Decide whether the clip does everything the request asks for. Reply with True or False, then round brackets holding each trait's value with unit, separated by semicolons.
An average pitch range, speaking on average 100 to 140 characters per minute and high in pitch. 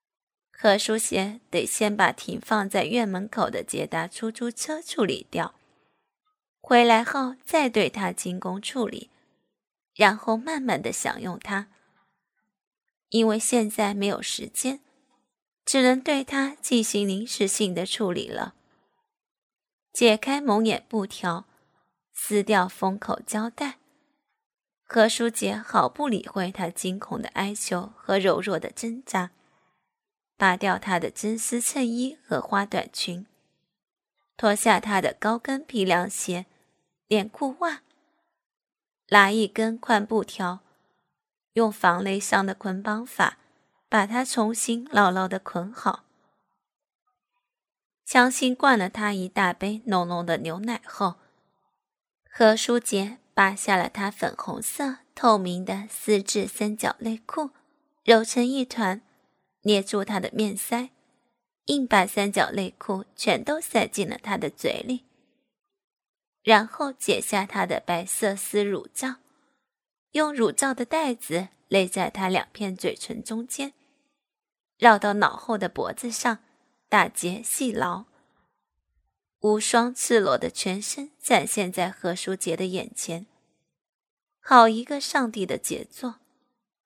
False (4.3 semitones; 180 characters per minute; 220 Hz)